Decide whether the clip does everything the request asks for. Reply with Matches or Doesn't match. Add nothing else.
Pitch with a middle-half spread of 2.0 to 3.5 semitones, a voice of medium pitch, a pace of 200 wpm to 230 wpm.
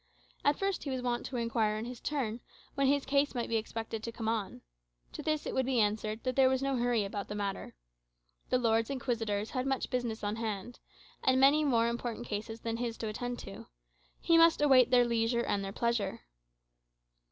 Doesn't match